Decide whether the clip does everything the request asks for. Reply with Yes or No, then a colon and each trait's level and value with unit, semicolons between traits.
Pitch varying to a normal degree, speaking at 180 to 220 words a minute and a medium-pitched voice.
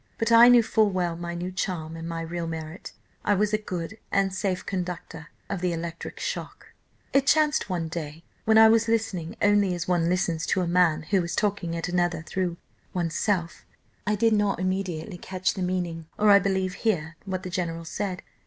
Yes: average, 3.3 semitones; average, 195 wpm; medium, 180 Hz